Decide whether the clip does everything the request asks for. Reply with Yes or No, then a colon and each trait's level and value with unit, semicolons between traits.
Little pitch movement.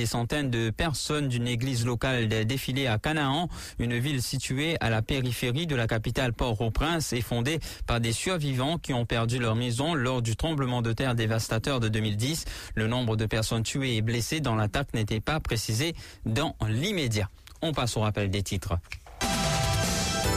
No: average, 3.7 semitones